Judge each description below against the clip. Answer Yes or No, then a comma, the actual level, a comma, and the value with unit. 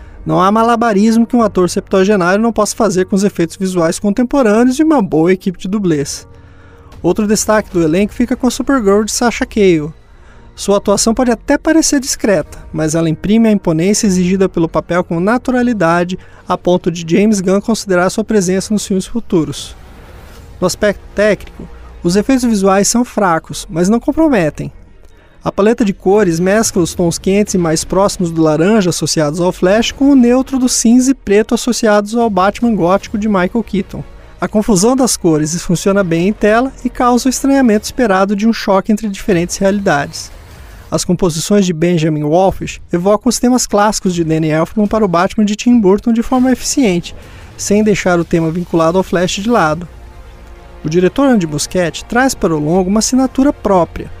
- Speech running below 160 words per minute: No, average, 175 wpm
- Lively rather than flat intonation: No, average, 4.8 semitones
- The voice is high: Yes, high, 195 Hz